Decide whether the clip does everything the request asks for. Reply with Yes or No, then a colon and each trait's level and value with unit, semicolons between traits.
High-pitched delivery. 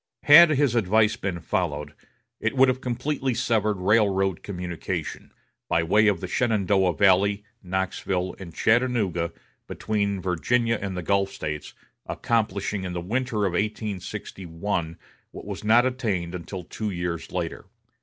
No: low, 100 Hz